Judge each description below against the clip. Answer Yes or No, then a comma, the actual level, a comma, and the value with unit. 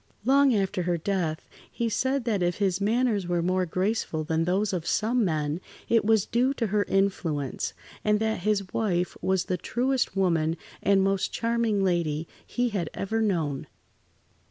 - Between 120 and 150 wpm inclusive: No, average, 165 wpm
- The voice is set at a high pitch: Yes, high, 195 Hz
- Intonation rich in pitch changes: No, average, 4.1 semitones